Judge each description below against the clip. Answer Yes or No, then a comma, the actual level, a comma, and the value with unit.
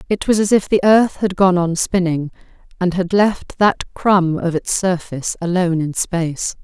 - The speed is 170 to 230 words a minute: Yes, average, 190 wpm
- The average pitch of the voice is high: No, medium, 180 Hz